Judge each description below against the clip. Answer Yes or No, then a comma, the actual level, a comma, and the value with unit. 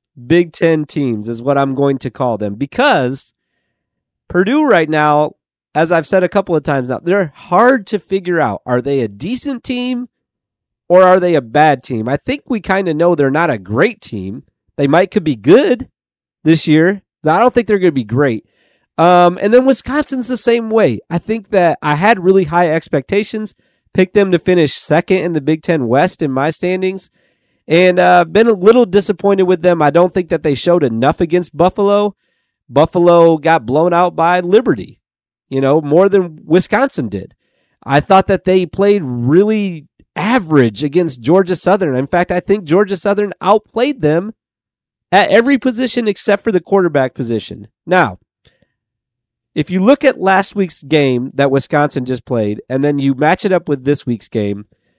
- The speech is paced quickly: No, average, 185 wpm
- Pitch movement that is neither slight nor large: No, wide, 5.9 semitones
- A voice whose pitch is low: No, medium, 175 Hz